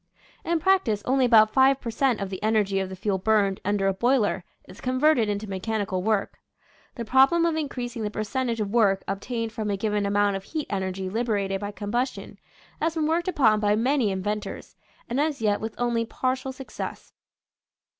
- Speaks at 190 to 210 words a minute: Yes, average, 195 wpm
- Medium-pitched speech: No, high, 220 Hz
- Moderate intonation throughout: Yes, average, 4.3 semitones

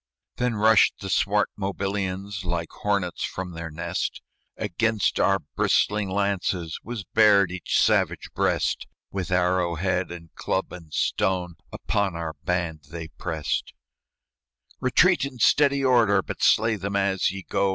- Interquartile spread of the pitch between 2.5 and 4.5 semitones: Yes, average, 2.8 semitones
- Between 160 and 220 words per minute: No, average, 140 wpm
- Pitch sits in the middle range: No, very low, 95 Hz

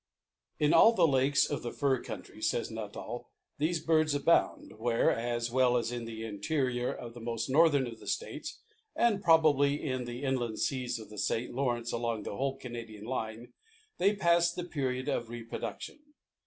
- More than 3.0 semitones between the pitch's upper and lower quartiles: Yes, average, 4.0 semitones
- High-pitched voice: No, low, 125 Hz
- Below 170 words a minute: No, average, 175 wpm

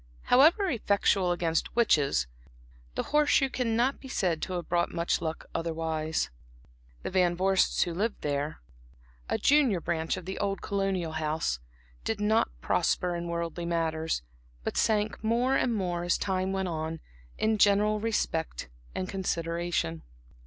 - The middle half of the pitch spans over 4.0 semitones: Yes, average, 4.4 semitones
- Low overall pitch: No, medium, 180 Hz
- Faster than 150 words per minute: No, average, 145 wpm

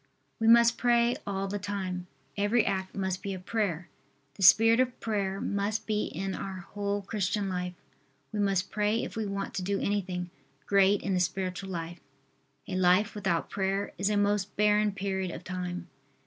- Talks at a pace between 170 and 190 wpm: Yes, average, 175 wpm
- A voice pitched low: No, high, 195 Hz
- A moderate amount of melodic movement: No, narrow, 1.9 semitones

